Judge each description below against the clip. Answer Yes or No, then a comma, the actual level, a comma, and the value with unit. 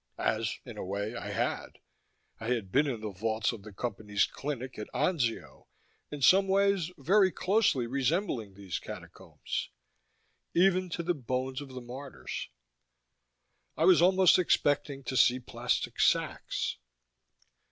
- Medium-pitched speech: No, low, 130 Hz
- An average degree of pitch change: No, wide, 7.7 semitones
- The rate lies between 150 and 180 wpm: No, average, 140 wpm